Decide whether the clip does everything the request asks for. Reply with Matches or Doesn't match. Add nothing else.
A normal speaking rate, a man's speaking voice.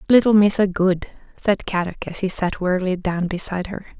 Doesn't match